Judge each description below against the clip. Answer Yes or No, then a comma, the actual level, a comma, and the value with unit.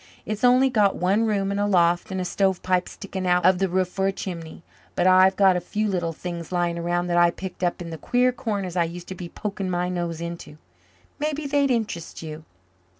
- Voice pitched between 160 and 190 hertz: Yes, medium, 185 Hz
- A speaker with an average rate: No, fast, 220 wpm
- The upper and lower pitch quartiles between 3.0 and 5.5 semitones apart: No, narrow, 2.6 semitones